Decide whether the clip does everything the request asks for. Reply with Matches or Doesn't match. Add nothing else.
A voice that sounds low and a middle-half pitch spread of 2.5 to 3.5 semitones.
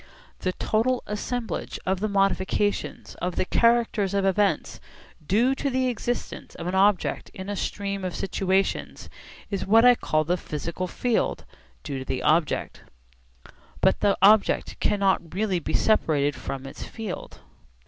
Doesn't match